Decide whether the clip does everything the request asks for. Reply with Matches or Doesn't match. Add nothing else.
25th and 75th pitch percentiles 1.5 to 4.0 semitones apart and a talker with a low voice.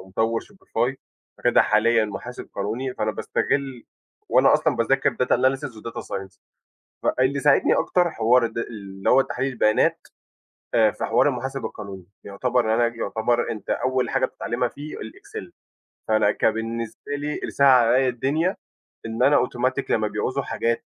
Matches